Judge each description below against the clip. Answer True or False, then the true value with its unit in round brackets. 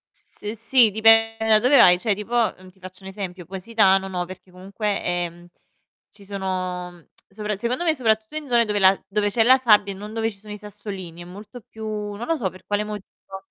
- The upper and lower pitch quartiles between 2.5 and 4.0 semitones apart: True (2.9 semitones)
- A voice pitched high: True (205 Hz)